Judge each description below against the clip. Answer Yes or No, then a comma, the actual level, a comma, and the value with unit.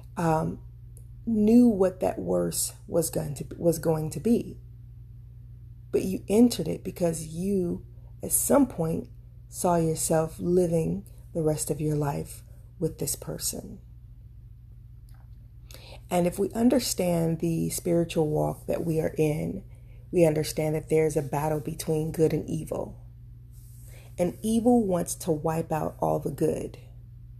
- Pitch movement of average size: No, wide, 6.1 semitones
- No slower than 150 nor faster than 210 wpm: No, slow, 135 wpm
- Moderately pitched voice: Yes, medium, 155 Hz